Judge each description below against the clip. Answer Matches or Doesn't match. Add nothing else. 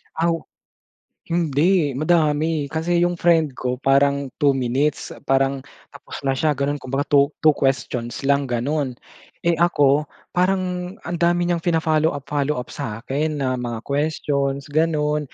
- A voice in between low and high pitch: Matches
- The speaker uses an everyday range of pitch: Matches